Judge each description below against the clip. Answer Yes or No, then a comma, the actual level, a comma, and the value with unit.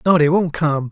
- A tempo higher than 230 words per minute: Yes, fast, 260 wpm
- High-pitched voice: No, medium, 160 Hz